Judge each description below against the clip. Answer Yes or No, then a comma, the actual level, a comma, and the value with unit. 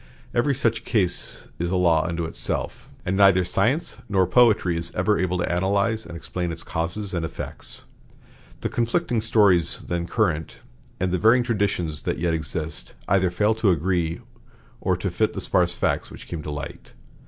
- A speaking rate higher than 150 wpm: Yes, average, 175 wpm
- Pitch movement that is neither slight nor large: Yes, average, 4.0 semitones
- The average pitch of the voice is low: Yes, very low, 90 Hz